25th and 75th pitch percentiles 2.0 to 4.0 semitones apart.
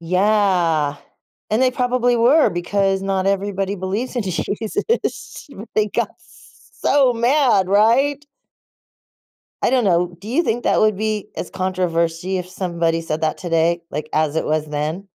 No: average, 5.0 semitones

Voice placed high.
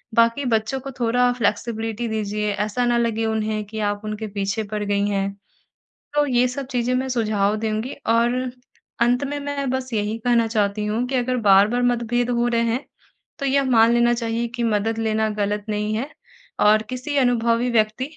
Yes: high, 230 Hz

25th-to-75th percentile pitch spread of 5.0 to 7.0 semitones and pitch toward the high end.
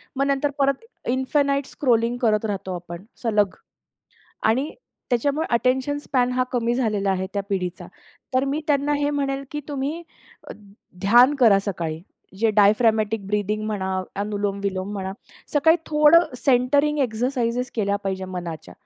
Yes: wide, 5.5 semitones; high, 235 Hz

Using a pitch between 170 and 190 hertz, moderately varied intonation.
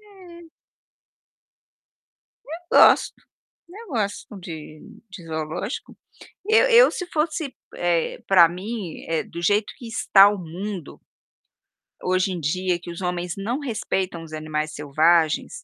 No: medium, 185 Hz; wide, 6.1 semitones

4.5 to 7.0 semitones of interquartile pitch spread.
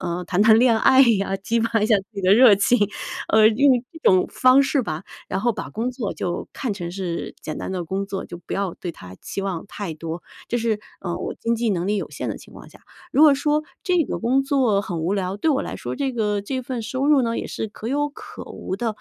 Yes: average, 4.9 semitones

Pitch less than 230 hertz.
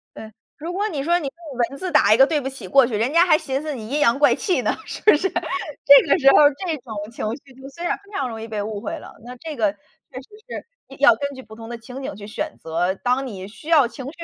No: very high, 265 Hz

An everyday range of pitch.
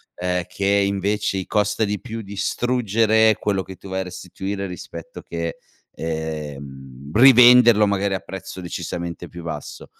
Yes: average, 3.5 semitones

